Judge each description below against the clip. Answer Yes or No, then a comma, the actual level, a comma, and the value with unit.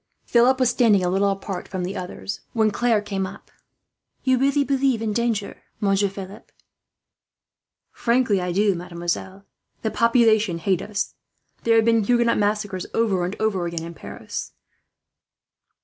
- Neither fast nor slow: Yes, average, 155 wpm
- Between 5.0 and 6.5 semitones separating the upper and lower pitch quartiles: No, average, 3.5 semitones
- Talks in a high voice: Yes, high, 205 Hz